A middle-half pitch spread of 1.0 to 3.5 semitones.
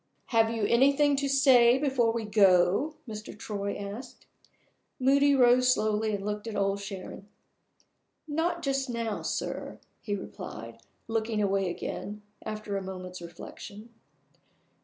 No: average, 4.3 semitones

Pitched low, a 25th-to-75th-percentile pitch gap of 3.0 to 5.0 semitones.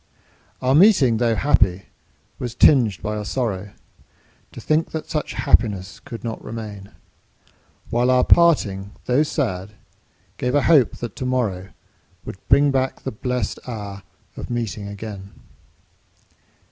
Yes: low, 115 Hz; average, 4.5 semitones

